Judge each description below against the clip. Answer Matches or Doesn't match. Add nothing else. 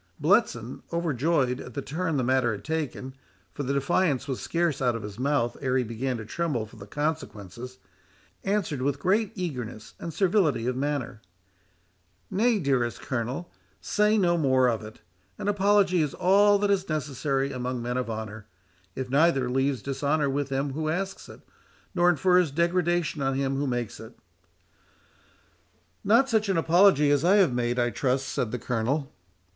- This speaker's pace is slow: Doesn't match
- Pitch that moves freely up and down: Matches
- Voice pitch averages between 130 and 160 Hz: Matches